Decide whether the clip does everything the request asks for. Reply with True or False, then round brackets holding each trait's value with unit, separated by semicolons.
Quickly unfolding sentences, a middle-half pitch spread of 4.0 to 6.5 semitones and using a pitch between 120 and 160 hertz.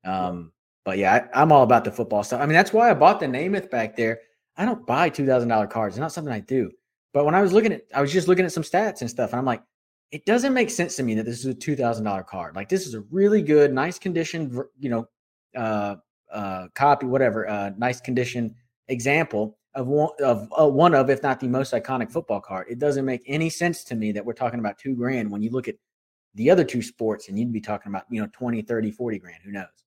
True (250 wpm; 5.3 semitones; 125 Hz)